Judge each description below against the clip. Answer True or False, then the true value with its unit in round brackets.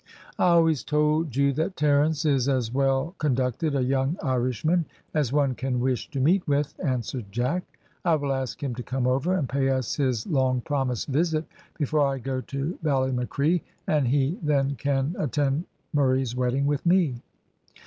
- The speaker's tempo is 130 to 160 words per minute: False (170 wpm)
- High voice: False (140 Hz)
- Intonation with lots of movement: False (2.7 semitones)